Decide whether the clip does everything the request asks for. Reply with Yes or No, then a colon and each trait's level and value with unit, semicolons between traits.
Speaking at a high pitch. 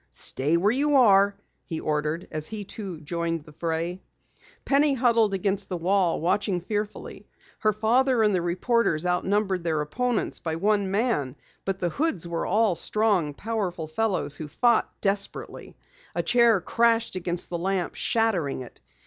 Yes: high, 195 Hz